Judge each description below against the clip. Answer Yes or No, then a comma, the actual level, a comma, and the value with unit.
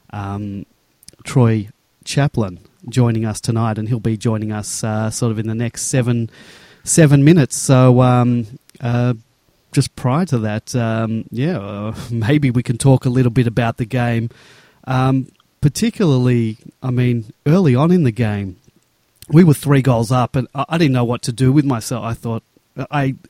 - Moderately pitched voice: No, low, 125 Hz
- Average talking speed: Yes, average, 175 wpm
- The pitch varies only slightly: No, average, 3.0 semitones